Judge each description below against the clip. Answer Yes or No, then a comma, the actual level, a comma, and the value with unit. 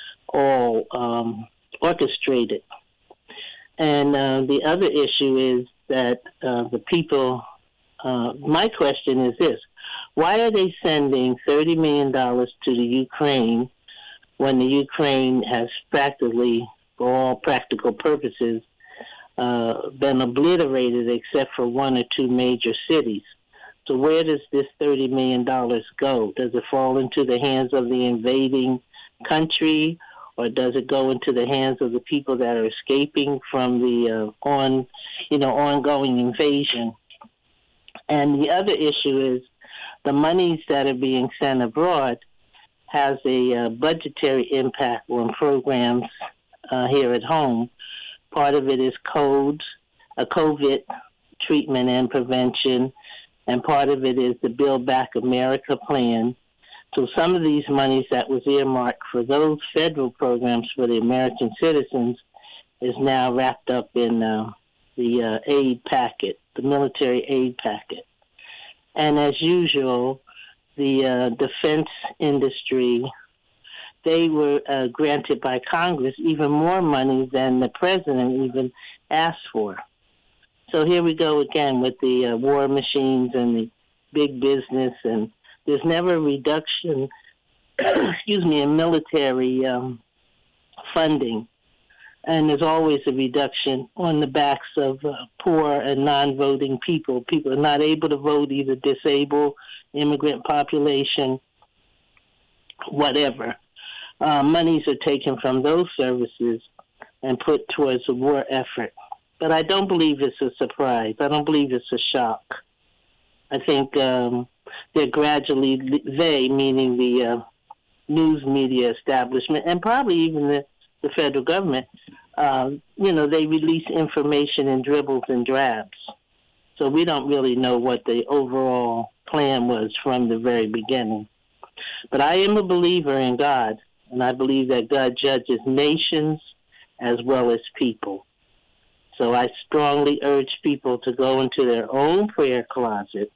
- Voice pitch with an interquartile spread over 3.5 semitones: No, average, 2.8 semitones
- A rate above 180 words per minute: No, slow, 135 wpm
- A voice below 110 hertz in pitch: No, low, 135 Hz